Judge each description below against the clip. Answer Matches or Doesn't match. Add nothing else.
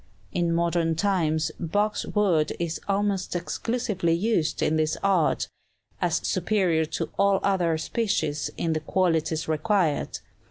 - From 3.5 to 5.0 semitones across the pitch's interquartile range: Matches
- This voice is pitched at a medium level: Matches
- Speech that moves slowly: Matches